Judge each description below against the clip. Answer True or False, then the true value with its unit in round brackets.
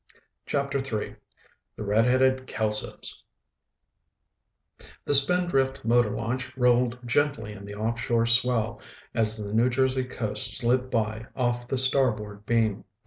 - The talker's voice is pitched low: True (120 Hz)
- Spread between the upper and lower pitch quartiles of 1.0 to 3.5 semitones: True (3.1 semitones)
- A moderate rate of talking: False (120 wpm)